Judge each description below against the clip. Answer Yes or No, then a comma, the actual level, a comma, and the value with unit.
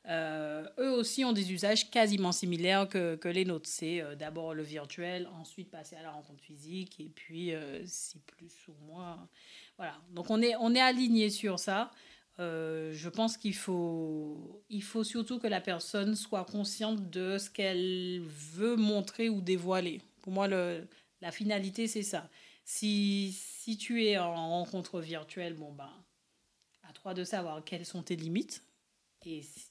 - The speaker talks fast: No, average, 170 wpm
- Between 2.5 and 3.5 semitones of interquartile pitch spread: No, average, 4.0 semitones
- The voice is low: No, medium, 185 Hz